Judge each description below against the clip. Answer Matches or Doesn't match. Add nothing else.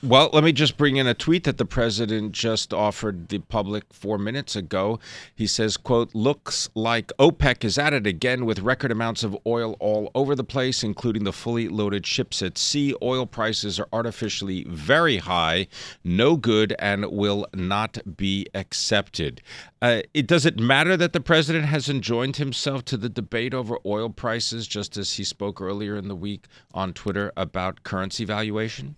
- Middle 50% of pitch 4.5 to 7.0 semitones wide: Doesn't match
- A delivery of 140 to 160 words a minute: Doesn't match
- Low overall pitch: Matches